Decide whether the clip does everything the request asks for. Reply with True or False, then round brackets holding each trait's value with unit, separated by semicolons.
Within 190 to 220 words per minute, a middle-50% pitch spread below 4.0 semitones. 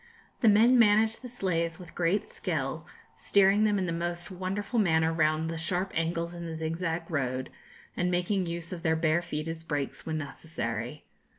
False (180 wpm; 2.9 semitones)